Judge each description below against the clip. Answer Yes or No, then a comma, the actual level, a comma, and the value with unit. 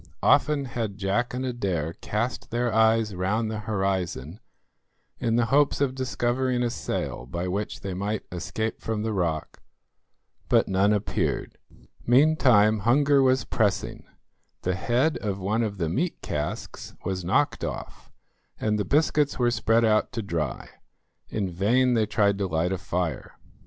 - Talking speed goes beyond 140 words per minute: Yes, average, 150 wpm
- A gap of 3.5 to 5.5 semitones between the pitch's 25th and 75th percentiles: Yes, average, 4.2 semitones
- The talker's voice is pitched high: No, low, 110 Hz